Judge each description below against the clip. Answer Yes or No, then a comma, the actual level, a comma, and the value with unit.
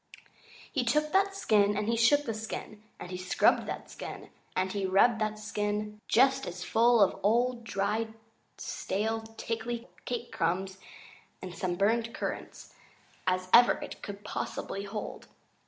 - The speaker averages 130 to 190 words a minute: Yes, average, 150 wpm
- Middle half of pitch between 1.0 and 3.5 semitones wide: Yes, average, 3.0 semitones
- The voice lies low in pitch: No, high, 215 Hz